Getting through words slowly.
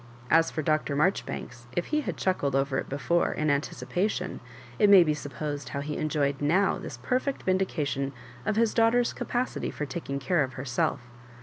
No: average, 185 wpm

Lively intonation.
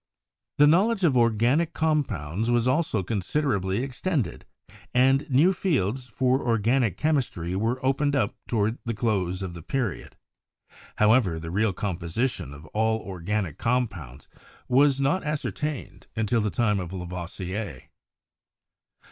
Yes: wide, 6.1 semitones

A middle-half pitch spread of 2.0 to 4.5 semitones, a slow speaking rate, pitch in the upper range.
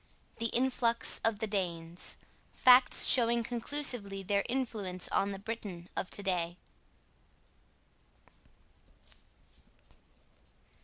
Yes: average, 4.0 semitones; slow, 90 wpm; high, 210 Hz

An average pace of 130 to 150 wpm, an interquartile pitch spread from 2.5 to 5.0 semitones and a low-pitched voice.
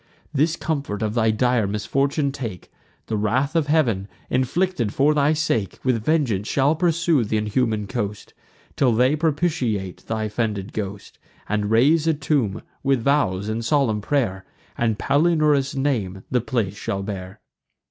No: average, 145 wpm; wide, 5.5 semitones; low, 120 Hz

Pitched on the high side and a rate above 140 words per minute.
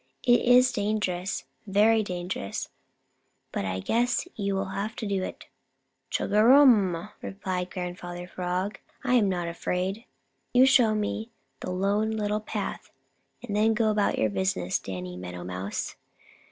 No: high, 200 Hz; slow, 135 wpm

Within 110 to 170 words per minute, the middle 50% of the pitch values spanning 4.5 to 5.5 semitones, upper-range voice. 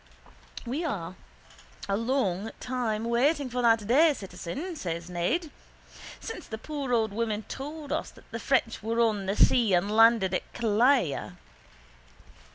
Yes: average, 145 wpm; average, 4.9 semitones; high, 230 Hz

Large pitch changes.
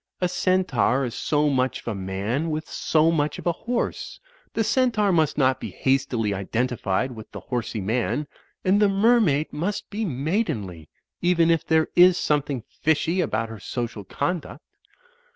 Yes: wide, 6.7 semitones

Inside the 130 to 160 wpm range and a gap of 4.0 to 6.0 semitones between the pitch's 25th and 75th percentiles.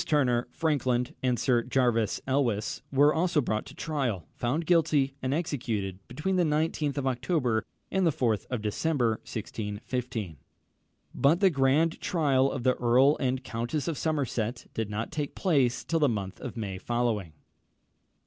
Yes: average, 155 wpm; average, 4.6 semitones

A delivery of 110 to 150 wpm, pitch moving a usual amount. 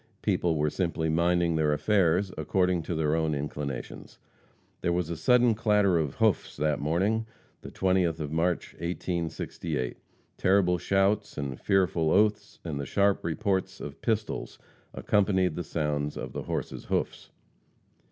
Yes: average, 140 wpm; average, 3.8 semitones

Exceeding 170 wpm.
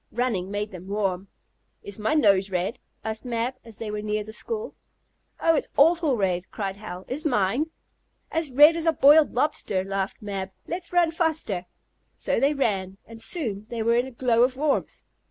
Yes: average, 185 wpm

